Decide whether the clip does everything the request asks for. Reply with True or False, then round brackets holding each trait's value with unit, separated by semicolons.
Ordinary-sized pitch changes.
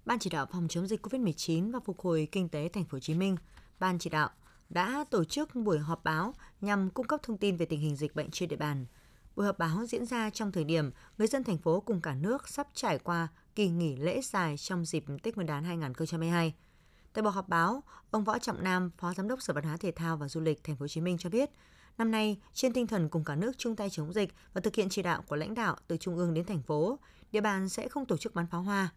True (4.9 semitones)